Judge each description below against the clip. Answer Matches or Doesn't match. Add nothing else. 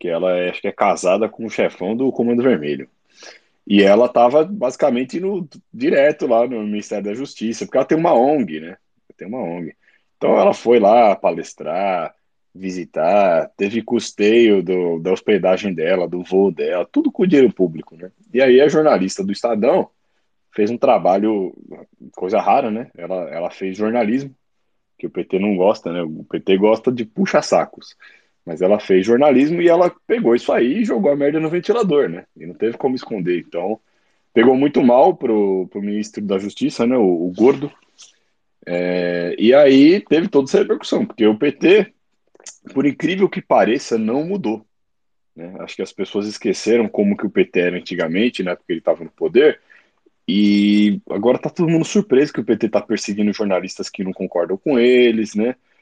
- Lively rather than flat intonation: Matches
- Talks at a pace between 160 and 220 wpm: Matches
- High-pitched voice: Doesn't match